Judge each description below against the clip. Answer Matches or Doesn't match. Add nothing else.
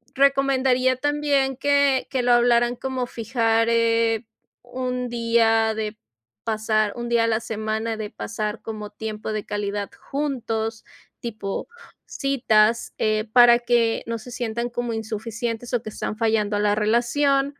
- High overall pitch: Matches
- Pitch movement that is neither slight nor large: Doesn't match